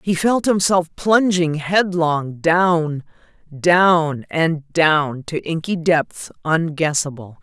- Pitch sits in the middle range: Yes, medium, 165 Hz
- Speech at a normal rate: No, slow, 105 wpm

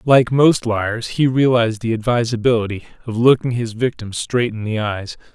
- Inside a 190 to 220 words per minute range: No, average, 170 wpm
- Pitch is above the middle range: No, low, 115 Hz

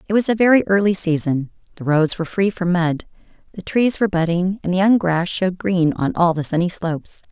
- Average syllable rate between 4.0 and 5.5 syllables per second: No, 5.8 syllables/s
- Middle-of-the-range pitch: Yes, medium, 180 Hz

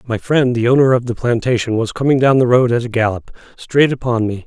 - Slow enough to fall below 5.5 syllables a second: No, 5.8 syllables/s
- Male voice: Yes, male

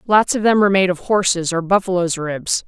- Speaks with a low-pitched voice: No, medium, 185 Hz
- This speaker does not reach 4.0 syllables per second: No, 5.5 syllables/s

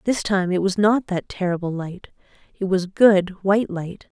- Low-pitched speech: No, high, 190 Hz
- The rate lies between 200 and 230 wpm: No, average, 185 wpm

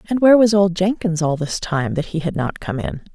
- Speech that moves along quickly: Yes, fast, 265 wpm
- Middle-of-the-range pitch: Yes, medium, 180 Hz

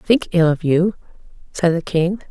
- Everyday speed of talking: Yes, average, 180 wpm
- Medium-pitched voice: Yes, medium, 175 Hz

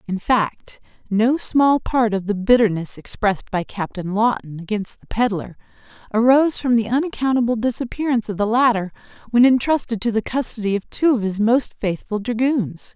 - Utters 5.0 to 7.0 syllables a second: Yes, 5.2 syllables/s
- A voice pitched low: No, high, 225 Hz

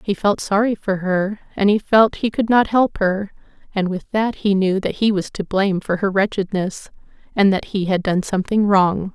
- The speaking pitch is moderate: No, high, 200 Hz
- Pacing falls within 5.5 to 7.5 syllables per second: No, 4.9 syllables/s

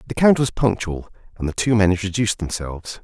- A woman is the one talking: No, male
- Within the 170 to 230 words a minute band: Yes, average, 200 wpm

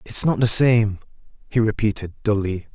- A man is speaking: Yes, male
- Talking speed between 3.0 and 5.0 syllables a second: Yes, 4.9 syllables/s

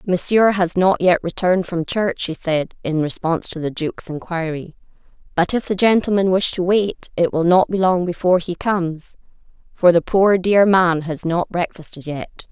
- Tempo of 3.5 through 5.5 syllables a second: Yes, 4.9 syllables/s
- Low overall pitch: No, medium, 180 Hz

